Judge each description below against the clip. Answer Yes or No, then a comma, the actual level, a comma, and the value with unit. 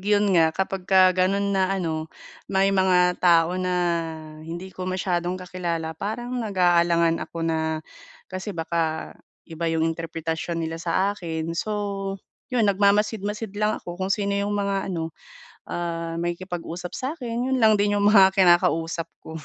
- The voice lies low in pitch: No, medium, 185 Hz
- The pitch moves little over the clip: No, average, 3.1 semitones